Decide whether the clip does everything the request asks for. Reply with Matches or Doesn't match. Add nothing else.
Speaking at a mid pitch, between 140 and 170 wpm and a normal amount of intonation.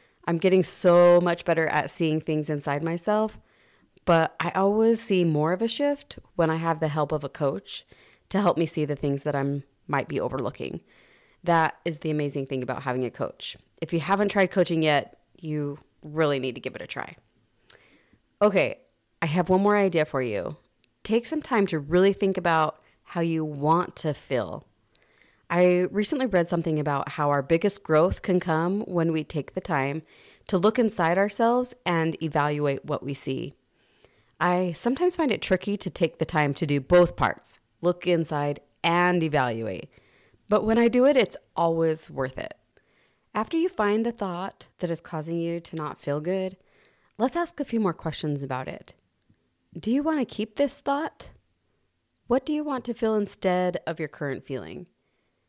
Doesn't match